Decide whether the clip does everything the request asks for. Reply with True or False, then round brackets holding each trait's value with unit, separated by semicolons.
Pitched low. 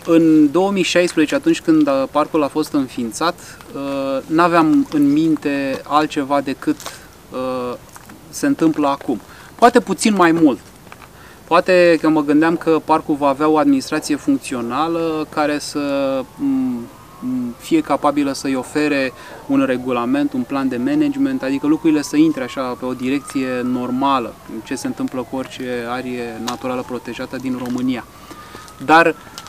False (155 Hz)